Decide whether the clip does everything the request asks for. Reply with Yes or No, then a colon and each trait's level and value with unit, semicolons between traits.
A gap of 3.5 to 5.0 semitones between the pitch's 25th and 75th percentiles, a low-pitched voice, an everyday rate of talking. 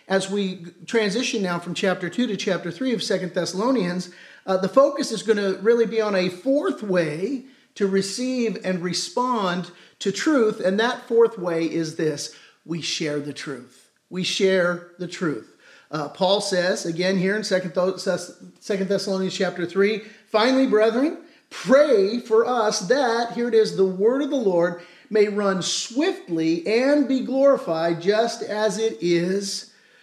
No: average, 4.5 semitones; high, 195 Hz; average, 160 wpm